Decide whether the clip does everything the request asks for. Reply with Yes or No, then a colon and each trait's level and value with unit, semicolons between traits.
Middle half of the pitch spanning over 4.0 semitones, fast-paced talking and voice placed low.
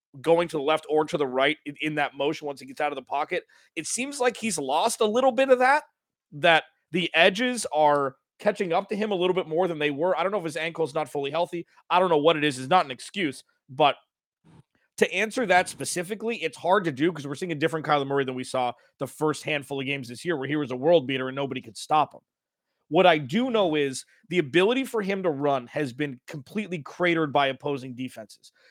No: average, 4.6 semitones; fast, 245 wpm; medium, 160 Hz